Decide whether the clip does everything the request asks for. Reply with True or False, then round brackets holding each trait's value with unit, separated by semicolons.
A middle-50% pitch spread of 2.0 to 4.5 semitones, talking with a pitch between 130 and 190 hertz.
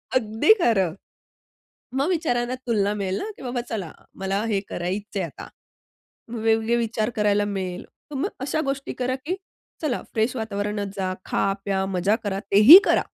False (3.8 semitones; 215 Hz)